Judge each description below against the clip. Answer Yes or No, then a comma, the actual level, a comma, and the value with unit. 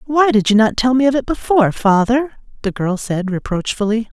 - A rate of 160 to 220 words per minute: Yes, average, 200 wpm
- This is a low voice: No, high, 230 Hz